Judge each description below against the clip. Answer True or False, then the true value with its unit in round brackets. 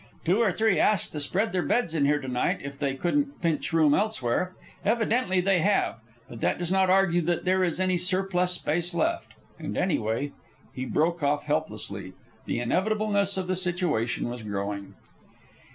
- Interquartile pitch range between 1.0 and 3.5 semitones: False (5.2 semitones)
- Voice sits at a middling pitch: True (175 Hz)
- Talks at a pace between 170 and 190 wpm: True (180 wpm)